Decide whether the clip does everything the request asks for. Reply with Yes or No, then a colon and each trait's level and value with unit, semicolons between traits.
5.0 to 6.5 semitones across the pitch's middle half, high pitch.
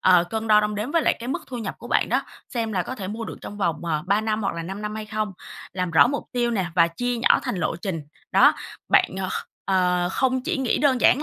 No: average, 4.6 semitones; high, 210 Hz